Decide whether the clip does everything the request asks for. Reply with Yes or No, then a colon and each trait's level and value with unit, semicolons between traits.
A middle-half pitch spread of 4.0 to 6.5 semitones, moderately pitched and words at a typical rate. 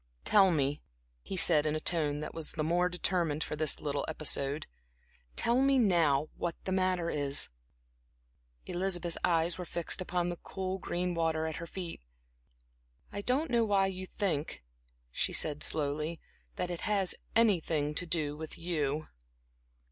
No: average, 3.4 semitones; medium, 170 Hz; average, 155 wpm